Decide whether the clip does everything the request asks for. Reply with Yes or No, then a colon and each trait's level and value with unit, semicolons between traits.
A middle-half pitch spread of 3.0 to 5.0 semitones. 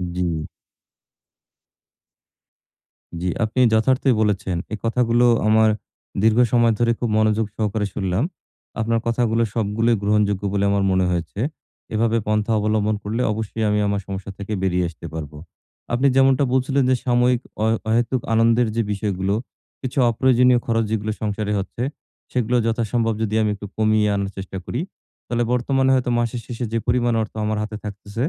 No: narrow, 2.6 semitones